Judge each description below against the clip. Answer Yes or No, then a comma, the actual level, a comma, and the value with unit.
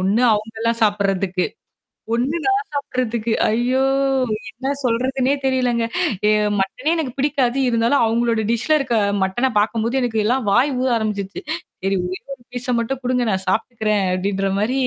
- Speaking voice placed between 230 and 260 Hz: Yes, high, 235 Hz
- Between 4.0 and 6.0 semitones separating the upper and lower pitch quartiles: No, average, 3.5 semitones